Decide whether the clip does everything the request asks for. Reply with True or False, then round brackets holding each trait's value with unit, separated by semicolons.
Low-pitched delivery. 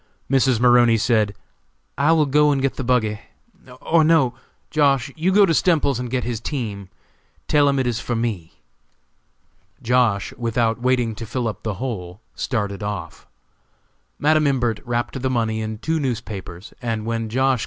True (120 Hz)